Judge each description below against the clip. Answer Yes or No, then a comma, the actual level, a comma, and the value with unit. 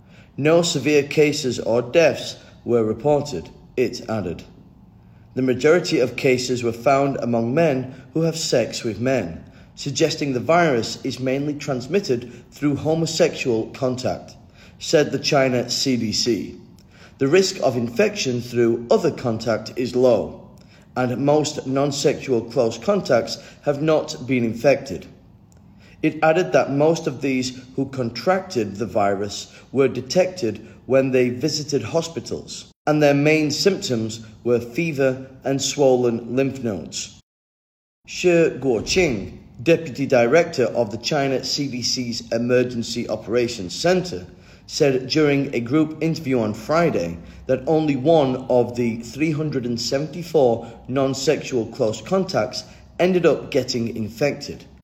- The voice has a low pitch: Yes, low, 130 Hz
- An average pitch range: Yes, average, 4.3 semitones